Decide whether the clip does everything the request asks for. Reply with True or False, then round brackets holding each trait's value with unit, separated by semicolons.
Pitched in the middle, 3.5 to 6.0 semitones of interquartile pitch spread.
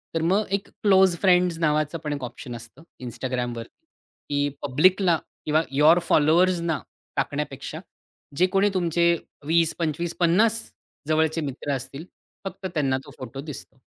True (160 Hz; 3.9 semitones)